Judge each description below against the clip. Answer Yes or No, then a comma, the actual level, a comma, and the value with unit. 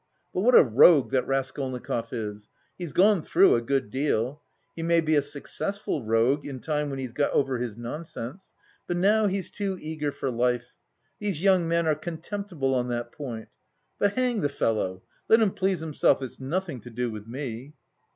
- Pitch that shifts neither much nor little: No, wide, 6.2 semitones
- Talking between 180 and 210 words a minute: Yes, average, 185 wpm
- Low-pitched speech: No, medium, 145 Hz